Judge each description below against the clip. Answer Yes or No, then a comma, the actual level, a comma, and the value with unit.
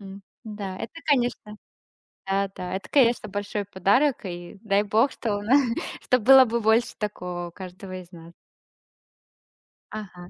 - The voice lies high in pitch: Yes, high, 205 Hz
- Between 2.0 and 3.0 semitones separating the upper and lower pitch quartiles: No, average, 3.7 semitones